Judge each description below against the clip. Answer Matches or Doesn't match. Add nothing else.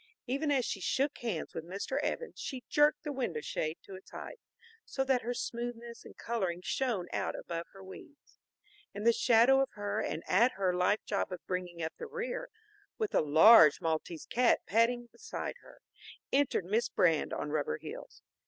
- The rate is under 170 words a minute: Doesn't match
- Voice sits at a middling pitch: Doesn't match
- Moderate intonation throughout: Doesn't match